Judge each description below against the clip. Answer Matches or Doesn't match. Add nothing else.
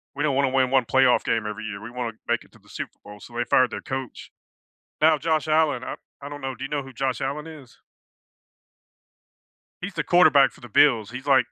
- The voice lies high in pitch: Doesn't match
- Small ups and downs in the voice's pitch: Doesn't match